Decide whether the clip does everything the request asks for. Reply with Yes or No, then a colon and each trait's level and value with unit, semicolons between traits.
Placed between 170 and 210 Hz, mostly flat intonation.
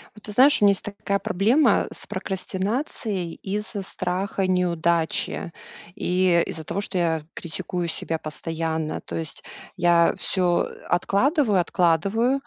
No: medium, 185 Hz; average, 3.3 semitones